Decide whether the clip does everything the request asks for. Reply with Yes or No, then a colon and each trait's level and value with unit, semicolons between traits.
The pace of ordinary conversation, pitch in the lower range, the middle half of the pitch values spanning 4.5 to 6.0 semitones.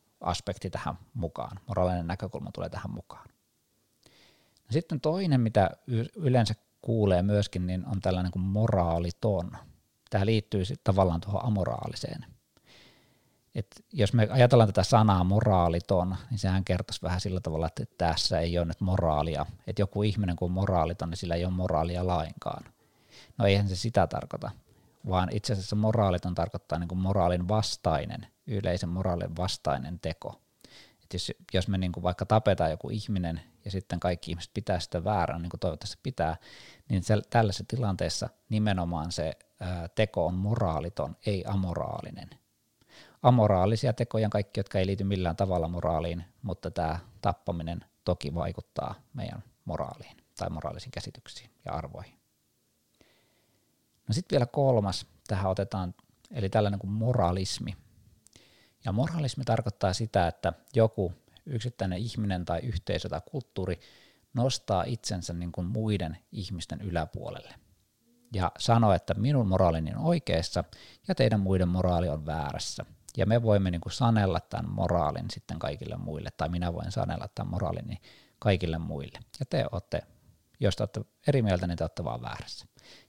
No: average, 145 wpm; very low, 95 Hz; average, 3.7 semitones